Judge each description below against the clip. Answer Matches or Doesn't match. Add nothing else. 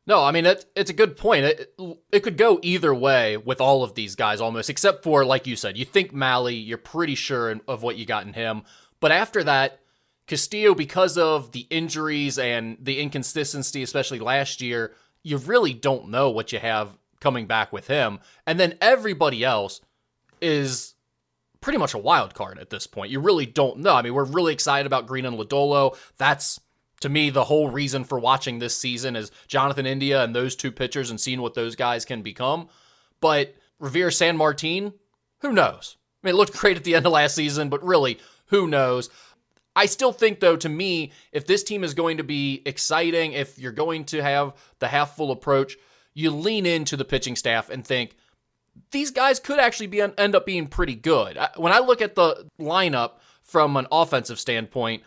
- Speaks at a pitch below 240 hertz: Matches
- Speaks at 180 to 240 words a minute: Matches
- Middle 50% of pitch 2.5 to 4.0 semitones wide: Doesn't match